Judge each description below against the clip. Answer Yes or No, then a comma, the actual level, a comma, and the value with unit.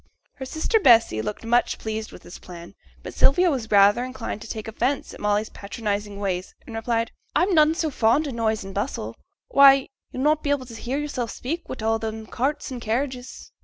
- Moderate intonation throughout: Yes, average, 4.2 semitones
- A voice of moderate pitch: No, high, 235 Hz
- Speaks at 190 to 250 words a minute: Yes, average, 200 wpm